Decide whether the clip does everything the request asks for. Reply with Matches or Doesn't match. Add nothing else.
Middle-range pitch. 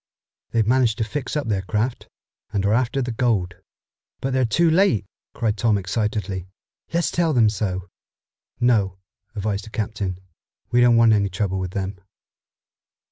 Doesn't match